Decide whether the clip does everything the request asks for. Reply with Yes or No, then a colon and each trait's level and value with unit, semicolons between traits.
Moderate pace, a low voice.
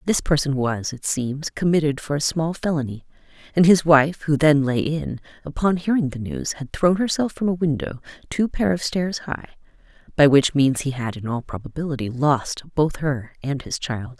No: average, 195 wpm; medium, 145 Hz